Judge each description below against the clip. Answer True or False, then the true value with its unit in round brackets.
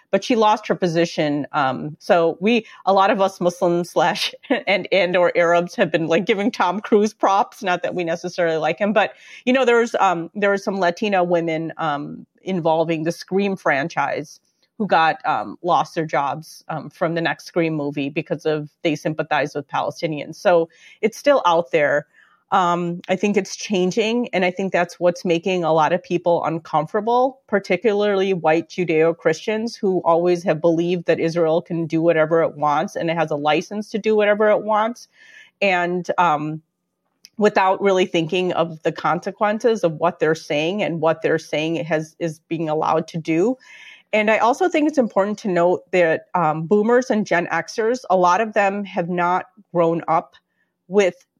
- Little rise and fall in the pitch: False (4.0 semitones)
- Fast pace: False (190 wpm)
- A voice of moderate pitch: True (175 Hz)